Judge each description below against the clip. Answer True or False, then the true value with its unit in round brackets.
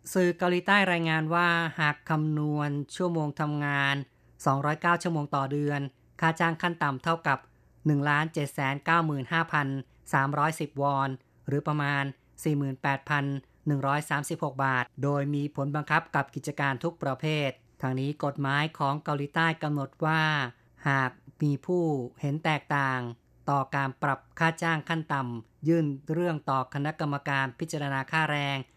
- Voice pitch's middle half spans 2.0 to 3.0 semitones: True (2.4 semitones)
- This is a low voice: False (145 Hz)